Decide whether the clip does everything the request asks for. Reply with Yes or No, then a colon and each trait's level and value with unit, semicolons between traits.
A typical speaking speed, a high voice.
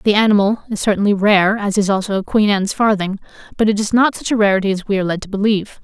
No: fast, 255 wpm; high, 205 Hz